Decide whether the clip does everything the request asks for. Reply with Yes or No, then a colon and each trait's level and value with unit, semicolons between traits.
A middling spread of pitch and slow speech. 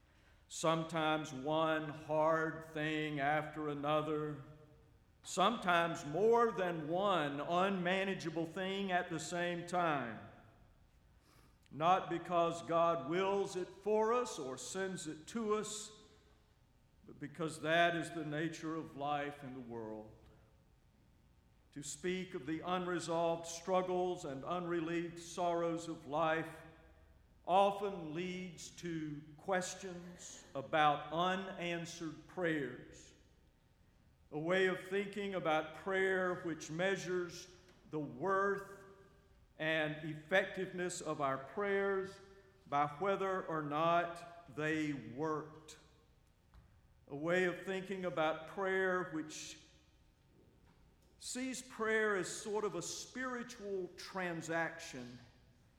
Yes: average, 3.3 semitones; slow, 100 wpm